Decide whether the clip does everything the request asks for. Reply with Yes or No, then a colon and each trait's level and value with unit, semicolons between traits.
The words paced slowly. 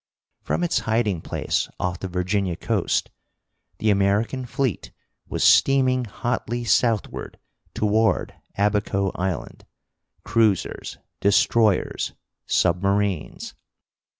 Yes: slow, 90 wpm